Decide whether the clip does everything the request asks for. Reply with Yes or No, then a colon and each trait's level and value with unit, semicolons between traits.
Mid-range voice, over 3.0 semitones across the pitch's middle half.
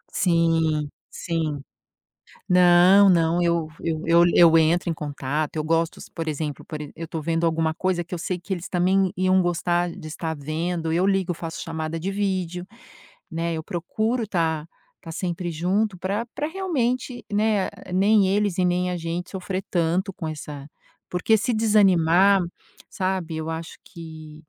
No: medium, 175 Hz; average, 2.7 semitones